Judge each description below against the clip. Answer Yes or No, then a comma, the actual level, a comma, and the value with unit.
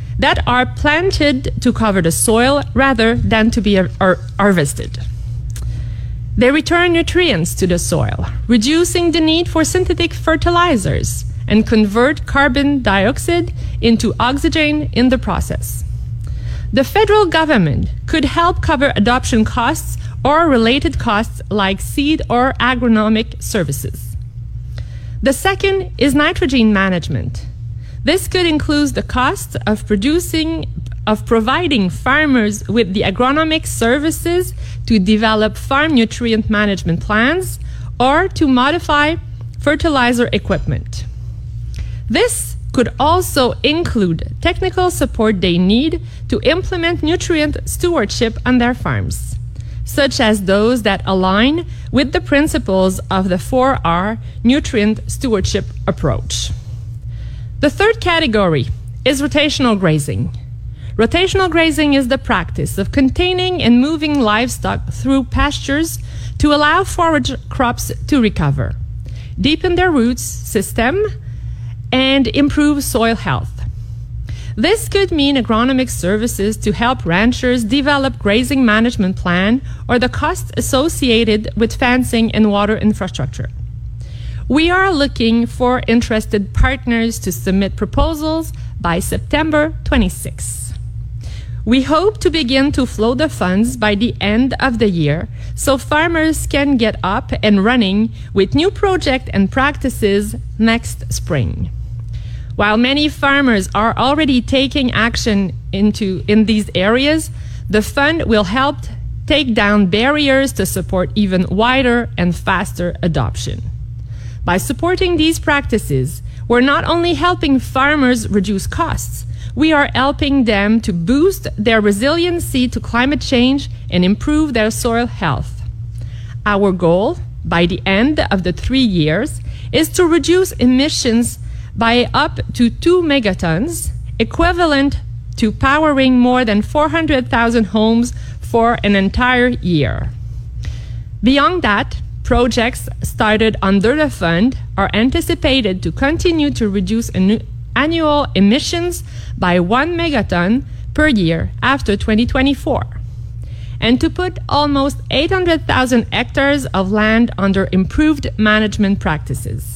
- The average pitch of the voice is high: Yes, high, 230 Hz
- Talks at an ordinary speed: No, slow, 120 wpm